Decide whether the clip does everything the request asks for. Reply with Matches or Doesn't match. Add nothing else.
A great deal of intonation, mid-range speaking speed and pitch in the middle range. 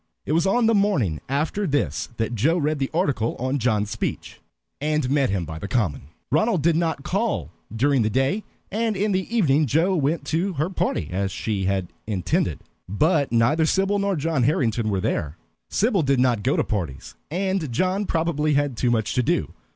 Matches